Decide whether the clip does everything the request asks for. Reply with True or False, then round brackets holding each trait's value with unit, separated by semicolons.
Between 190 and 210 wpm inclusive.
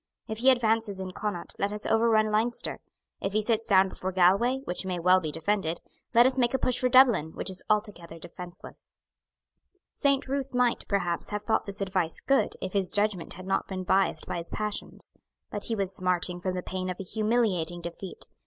True (200 wpm)